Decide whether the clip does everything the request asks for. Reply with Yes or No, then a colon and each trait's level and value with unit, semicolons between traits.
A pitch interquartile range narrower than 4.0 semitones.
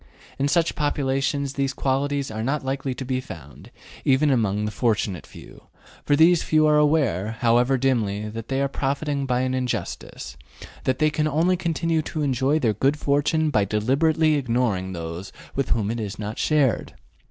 No: average, 4.7 semitones